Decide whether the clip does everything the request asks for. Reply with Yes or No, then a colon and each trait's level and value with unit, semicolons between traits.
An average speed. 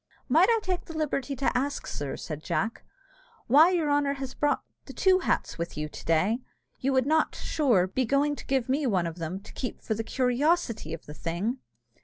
No: fast, 210 wpm